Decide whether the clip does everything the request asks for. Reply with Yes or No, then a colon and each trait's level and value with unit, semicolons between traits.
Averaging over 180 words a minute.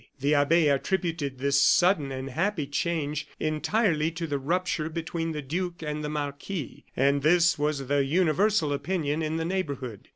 No: average, 160 wpm